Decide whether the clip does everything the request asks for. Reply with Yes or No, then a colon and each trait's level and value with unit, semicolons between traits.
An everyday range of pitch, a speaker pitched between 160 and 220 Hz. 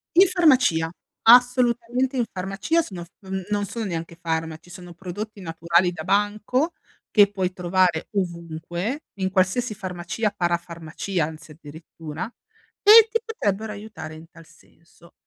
Yes: average, 4.9 semitones; medium, 185 Hz